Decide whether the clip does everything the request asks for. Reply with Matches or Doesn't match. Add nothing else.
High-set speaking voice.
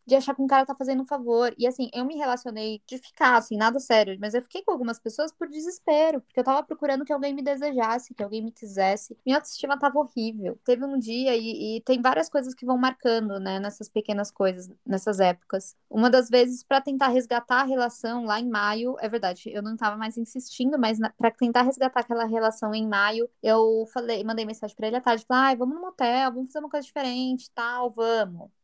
Matches